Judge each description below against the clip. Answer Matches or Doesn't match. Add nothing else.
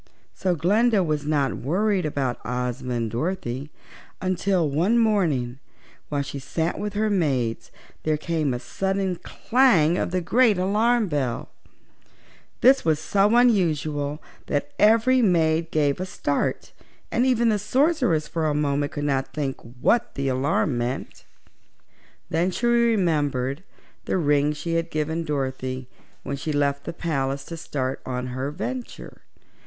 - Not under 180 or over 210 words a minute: Doesn't match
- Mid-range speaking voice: Matches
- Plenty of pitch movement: Matches